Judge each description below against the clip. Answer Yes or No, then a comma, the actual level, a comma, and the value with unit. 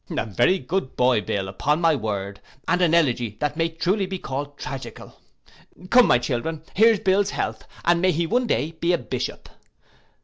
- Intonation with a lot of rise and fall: Yes, wide, 6.7 semitones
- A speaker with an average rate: Yes, average, 180 wpm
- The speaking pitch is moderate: Yes, medium, 160 Hz